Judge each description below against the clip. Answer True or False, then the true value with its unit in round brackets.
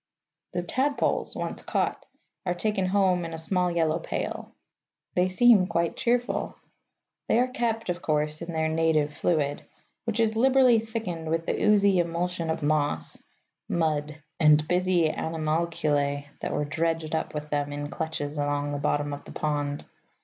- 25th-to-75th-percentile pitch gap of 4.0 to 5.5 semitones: False (3.6 semitones)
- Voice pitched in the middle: True (165 Hz)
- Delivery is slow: False (155 wpm)